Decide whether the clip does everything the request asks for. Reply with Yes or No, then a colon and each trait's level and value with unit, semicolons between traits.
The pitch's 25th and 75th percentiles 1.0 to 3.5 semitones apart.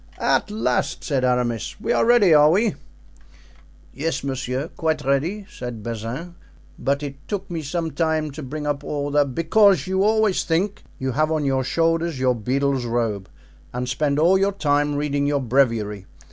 No: average, 4.1 semitones